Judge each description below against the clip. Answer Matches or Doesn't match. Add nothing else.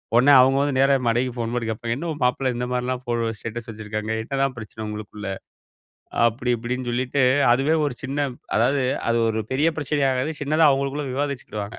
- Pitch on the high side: Doesn't match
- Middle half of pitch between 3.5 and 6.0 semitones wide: Doesn't match